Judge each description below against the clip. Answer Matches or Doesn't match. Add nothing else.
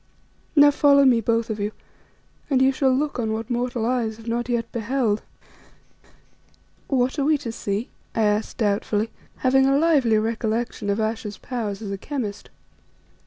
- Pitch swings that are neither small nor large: Matches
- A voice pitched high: Matches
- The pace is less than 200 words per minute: Matches